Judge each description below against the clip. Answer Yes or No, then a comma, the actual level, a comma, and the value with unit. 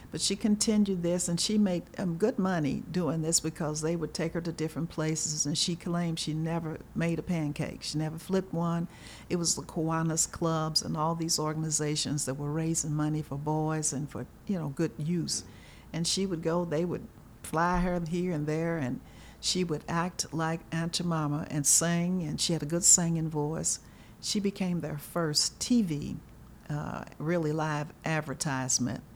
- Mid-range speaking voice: Yes, medium, 160 Hz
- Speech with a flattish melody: Yes, narrow, 2.2 semitones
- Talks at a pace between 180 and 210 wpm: Yes, average, 185 wpm